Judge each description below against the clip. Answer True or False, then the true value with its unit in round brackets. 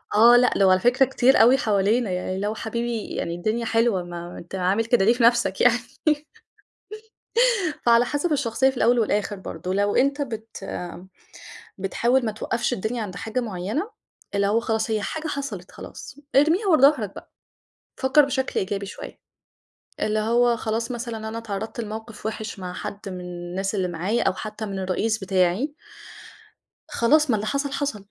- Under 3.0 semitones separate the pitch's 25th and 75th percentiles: False (3.7 semitones)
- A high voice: True (220 Hz)